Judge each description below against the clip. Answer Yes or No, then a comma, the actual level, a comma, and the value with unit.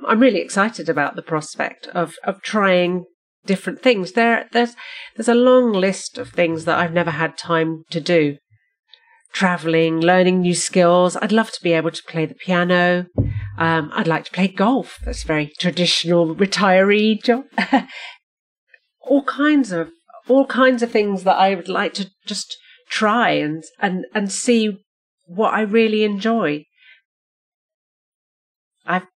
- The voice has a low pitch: No, high, 190 Hz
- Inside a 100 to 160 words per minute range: Yes, average, 150 wpm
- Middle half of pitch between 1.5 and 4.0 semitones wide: No, average, 5.0 semitones